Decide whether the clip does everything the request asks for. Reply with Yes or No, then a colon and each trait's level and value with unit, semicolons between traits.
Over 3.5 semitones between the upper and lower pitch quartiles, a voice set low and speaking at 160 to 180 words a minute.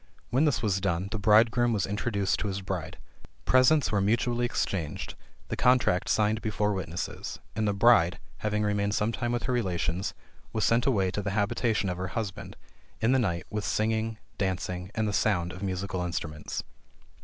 No: average, 3.2 semitones; low, 105 Hz; average, 175 wpm